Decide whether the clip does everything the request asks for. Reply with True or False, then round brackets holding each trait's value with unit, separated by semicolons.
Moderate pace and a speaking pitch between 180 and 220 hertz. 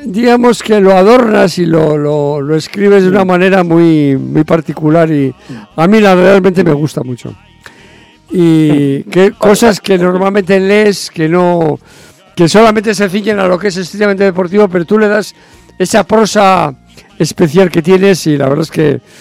True (170 wpm; 185 Hz)